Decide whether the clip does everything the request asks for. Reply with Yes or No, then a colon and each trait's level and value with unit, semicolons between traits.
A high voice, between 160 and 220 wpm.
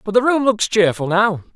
No: high, 205 Hz; fast, 230 wpm